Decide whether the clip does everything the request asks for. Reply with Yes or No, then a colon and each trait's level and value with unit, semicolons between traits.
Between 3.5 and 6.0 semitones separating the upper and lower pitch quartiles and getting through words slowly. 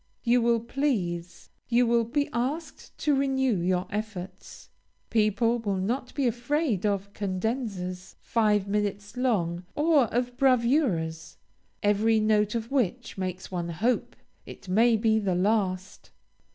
Yes: average, 4.4 semitones; slow, 130 wpm